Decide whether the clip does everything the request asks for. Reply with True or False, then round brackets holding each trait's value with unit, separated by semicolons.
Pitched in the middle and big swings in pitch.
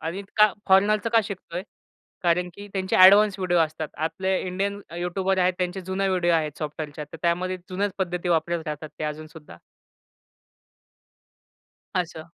False (180 Hz; 2.9 semitones)